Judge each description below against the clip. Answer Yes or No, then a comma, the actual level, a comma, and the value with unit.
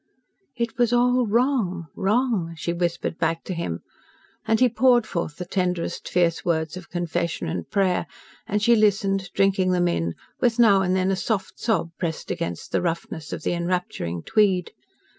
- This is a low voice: No, medium, 185 Hz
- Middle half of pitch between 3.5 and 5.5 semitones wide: Yes, average, 4.3 semitones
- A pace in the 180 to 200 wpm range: No, average, 170 wpm